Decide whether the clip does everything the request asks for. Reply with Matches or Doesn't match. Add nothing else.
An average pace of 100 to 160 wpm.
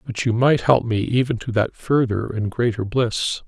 Doesn't match